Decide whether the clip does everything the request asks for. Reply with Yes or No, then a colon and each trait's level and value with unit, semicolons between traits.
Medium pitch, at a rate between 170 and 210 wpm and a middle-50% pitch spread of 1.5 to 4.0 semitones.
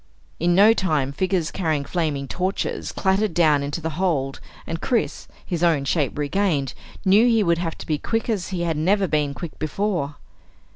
No: medium, 170 Hz; average, 180 wpm; average, 4.4 semitones